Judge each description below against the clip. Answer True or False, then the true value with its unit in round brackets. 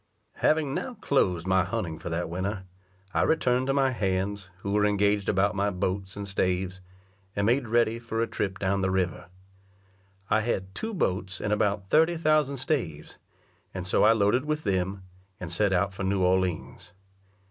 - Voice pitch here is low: True (100 Hz)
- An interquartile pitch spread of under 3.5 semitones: False (3.9 semitones)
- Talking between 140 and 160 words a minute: False (175 wpm)